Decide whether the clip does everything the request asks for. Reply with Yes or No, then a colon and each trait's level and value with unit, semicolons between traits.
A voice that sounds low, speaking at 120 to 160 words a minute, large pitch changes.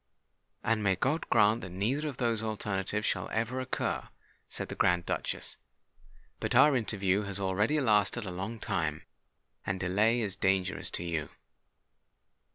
No: low, 105 Hz; average, 150 wpm; average, 3.5 semitones